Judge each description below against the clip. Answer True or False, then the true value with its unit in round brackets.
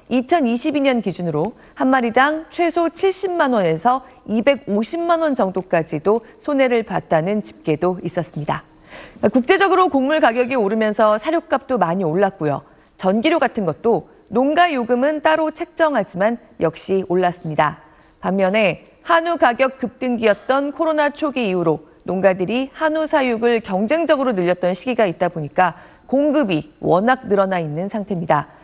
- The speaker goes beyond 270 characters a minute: True (305 characters per minute)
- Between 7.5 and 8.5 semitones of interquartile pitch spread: True (8.1 semitones)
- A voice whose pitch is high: True (230 Hz)